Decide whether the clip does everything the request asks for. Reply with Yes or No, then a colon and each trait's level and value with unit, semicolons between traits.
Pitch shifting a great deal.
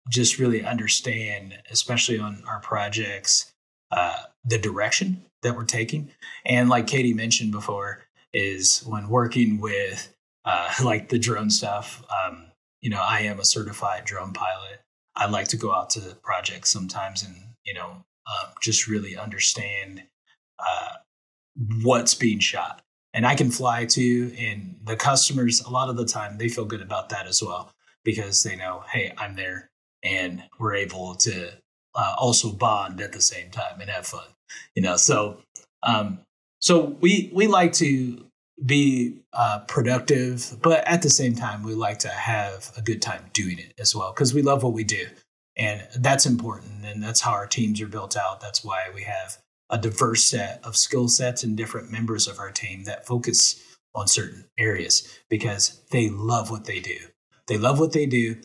No: average, 3.0 semitones